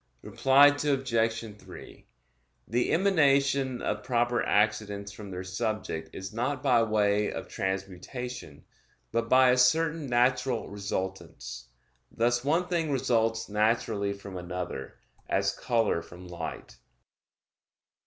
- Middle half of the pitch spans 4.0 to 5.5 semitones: Yes, average, 4.6 semitones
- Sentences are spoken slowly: Yes, slow, 115 wpm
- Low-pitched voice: Yes, low, 115 Hz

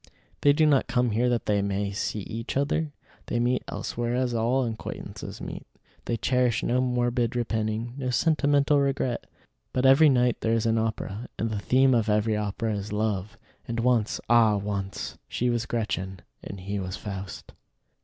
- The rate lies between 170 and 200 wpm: Yes, average, 175 wpm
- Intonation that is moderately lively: Yes, average, 3.1 semitones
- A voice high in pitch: No, low, 115 Hz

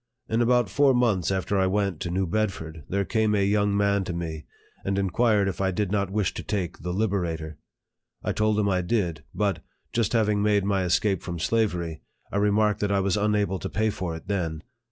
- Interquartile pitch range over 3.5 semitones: No, average, 2.9 semitones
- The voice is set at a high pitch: No, low, 100 Hz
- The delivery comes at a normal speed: No, fast, 215 wpm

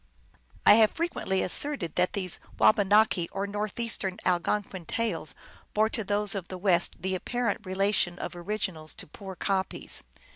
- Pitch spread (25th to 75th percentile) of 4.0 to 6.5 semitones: No, narrow, 2.6 semitones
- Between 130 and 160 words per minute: Yes, average, 145 wpm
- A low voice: No, high, 195 Hz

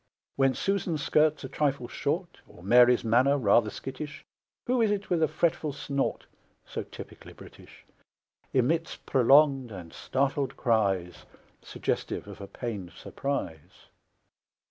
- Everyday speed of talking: No, slow, 125 wpm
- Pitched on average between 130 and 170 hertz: Yes, low, 135 Hz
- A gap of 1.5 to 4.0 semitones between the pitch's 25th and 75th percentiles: No, average, 4.7 semitones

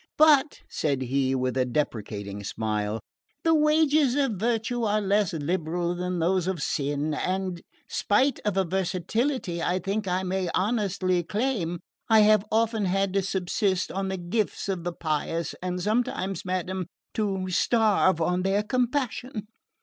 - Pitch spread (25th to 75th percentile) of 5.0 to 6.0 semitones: No, average, 4.0 semitones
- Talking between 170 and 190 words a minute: No, average, 150 wpm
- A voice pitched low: No, high, 190 Hz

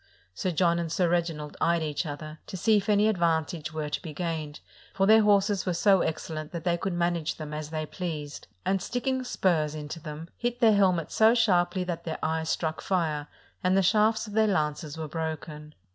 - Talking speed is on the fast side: Yes, fast, 210 wpm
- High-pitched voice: No, medium, 170 Hz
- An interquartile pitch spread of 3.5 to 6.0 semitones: Yes, average, 3.9 semitones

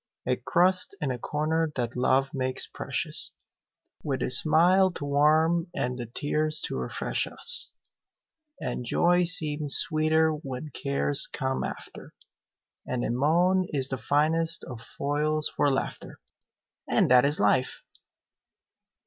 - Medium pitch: Yes, medium, 150 Hz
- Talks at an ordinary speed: No, slow, 130 wpm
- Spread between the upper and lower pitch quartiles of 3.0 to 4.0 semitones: Yes, average, 3.5 semitones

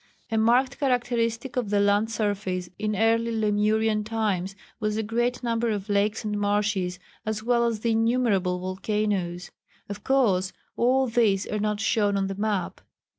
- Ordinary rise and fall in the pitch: No, narrow, 2.3 semitones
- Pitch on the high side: Yes, high, 215 Hz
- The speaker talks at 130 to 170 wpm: Yes, average, 160 wpm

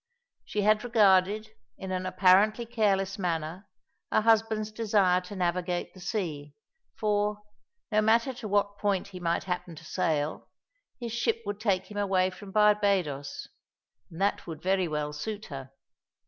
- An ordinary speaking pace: Yes, average, 150 wpm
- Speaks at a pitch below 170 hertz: No, high, 195 Hz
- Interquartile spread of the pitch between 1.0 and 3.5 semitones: Yes, average, 3.0 semitones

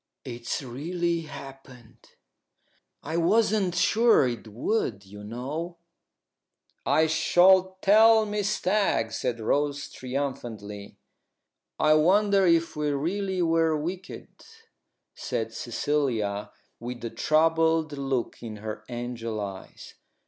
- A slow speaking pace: Yes, slow, 105 wpm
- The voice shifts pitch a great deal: Yes, wide, 6.8 semitones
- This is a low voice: No, medium, 150 Hz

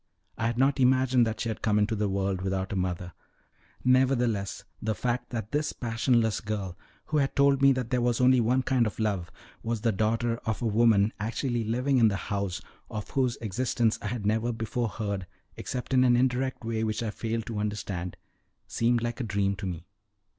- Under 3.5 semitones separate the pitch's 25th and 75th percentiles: Yes, average, 3.0 semitones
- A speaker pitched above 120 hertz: No, low, 115 Hz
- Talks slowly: No, average, 200 wpm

